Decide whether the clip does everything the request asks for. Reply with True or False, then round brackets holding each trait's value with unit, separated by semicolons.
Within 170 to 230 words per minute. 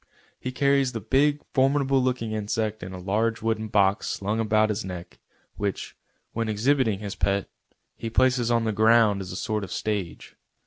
True (175 wpm)